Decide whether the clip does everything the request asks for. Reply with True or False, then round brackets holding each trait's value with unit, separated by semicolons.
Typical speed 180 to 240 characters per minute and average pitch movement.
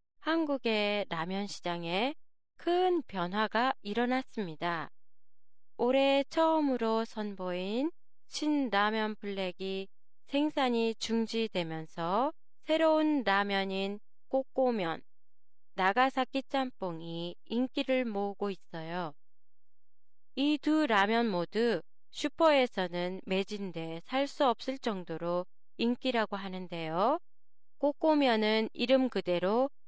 False (210 characters per minute; 5.9 semitones)